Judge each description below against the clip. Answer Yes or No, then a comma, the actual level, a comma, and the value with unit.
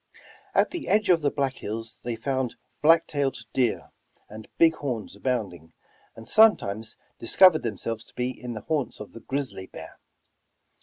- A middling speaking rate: Yes, average, 160 wpm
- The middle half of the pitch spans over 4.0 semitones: Yes, average, 4.8 semitones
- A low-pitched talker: Yes, low, 125 Hz